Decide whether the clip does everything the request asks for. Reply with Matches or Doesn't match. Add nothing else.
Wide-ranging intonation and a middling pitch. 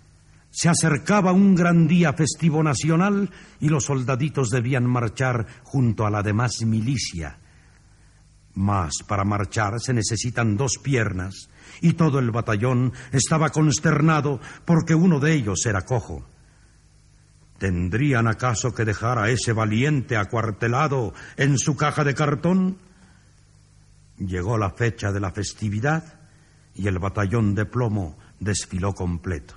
Doesn't match